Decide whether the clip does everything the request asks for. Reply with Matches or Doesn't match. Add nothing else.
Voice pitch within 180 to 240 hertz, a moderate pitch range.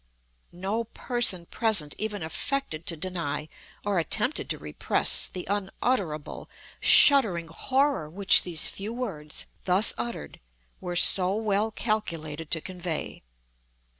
Matches